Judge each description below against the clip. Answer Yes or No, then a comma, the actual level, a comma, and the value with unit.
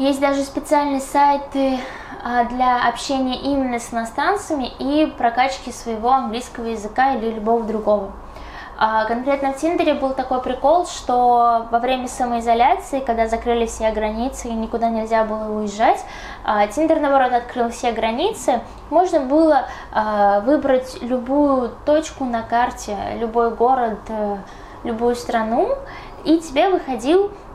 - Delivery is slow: No, average, 120 wpm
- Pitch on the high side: Yes, very high, 250 Hz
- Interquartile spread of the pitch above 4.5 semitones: No, average, 3.4 semitones